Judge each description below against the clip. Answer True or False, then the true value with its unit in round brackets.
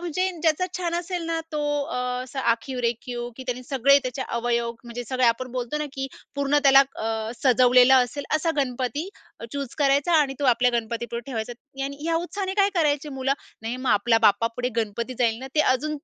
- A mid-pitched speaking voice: False (260 Hz)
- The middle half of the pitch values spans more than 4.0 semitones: False (3.7 semitones)